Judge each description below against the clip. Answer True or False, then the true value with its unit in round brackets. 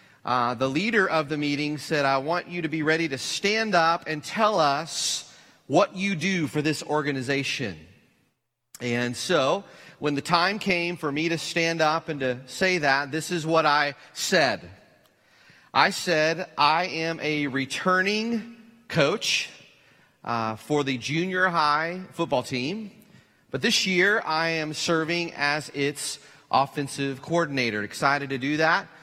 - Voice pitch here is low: False (155 Hz)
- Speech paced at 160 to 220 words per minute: False (150 wpm)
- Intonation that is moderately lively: True (3.8 semitones)